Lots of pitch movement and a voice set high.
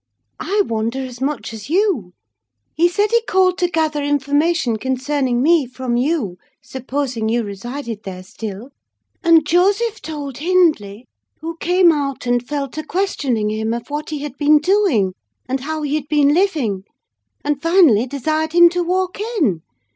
Yes: wide, 5.9 semitones; very high, 290 Hz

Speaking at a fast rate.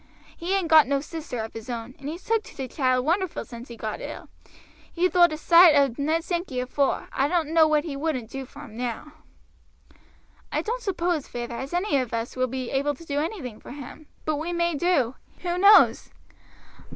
Yes: fast, 210 wpm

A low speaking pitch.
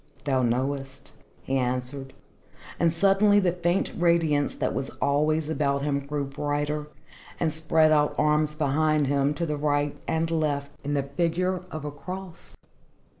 No: medium, 150 Hz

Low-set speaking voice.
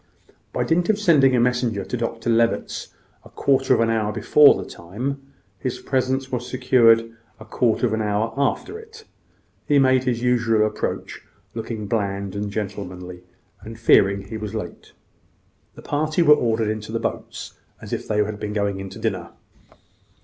Yes: low, 115 Hz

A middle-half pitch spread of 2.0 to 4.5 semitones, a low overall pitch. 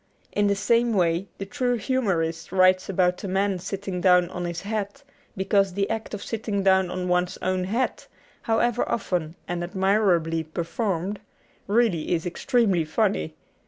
No: average, 2.9 semitones; high, 190 Hz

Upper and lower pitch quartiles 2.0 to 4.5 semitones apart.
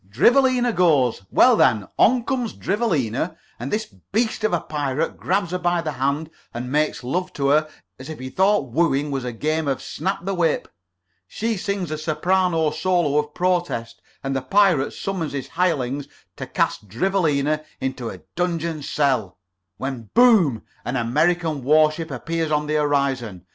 No: average, 5.1 semitones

